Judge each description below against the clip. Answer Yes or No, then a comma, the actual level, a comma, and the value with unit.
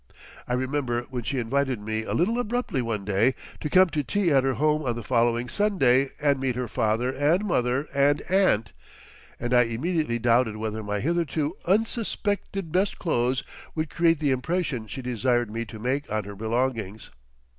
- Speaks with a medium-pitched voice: No, low, 130 Hz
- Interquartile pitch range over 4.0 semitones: Yes, average, 5.2 semitones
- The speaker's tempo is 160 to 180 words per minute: Yes, average, 175 wpm